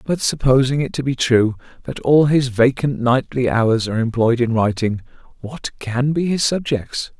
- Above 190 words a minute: No, average, 175 wpm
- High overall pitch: No, low, 125 Hz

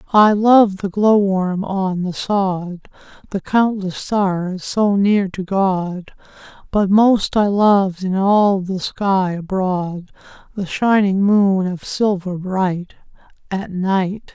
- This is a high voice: Yes, high, 195 Hz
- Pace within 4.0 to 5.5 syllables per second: No, 3.1 syllables/s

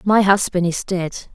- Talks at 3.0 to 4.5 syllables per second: Yes, 4.2 syllables/s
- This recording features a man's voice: No, female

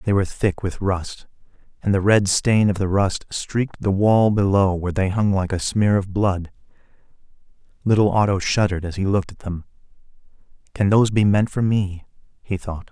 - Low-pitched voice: Yes, low, 100 Hz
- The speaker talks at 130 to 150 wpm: No, average, 185 wpm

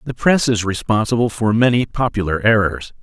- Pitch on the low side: Yes, low, 110 Hz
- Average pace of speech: Yes, average, 160 wpm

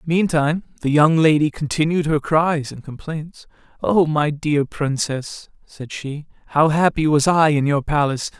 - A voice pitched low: No, medium, 150 Hz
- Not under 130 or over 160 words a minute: Yes, average, 155 wpm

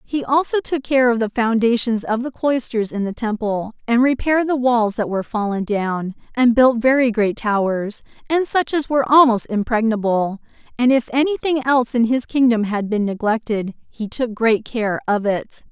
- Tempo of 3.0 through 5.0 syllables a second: Yes, 4.9 syllables/s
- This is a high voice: Yes, high, 235 Hz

